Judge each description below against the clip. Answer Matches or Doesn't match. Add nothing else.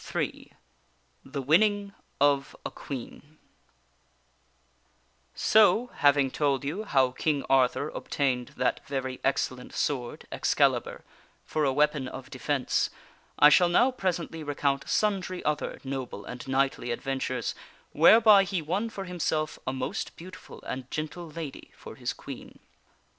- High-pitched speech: Doesn't match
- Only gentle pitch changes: Doesn't match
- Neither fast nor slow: Doesn't match